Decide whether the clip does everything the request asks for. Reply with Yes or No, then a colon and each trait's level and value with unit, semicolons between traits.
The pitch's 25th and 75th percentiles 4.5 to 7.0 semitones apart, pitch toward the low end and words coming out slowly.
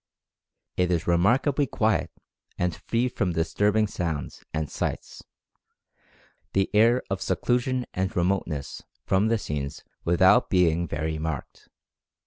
Yes: average, 5.2 semitones; very low, 95 Hz; slow, 115 wpm